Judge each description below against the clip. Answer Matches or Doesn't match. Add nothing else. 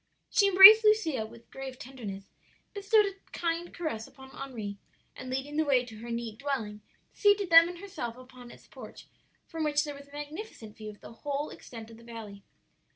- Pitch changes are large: Matches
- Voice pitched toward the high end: Matches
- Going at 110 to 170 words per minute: Doesn't match